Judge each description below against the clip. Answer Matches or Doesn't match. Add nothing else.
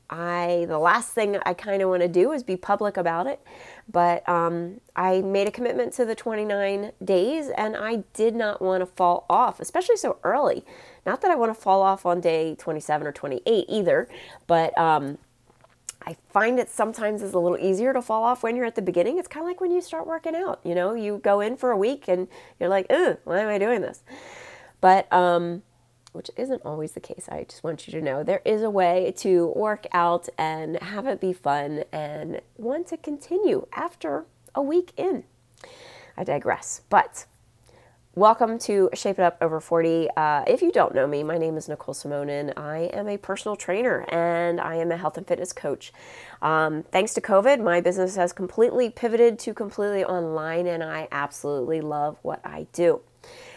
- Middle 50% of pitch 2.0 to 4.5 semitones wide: Doesn't match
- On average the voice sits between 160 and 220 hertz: Matches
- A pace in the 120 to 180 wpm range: Doesn't match